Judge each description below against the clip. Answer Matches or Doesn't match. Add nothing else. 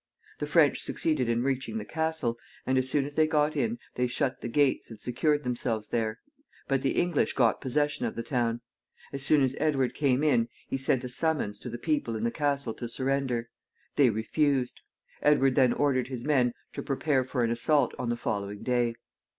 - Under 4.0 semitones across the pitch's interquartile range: Matches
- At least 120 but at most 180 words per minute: Doesn't match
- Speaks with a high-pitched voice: Doesn't match